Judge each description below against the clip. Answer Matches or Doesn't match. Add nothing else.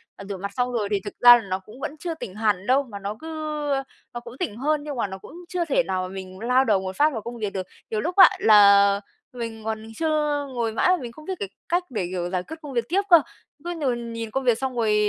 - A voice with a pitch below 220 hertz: Doesn't match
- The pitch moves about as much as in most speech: Doesn't match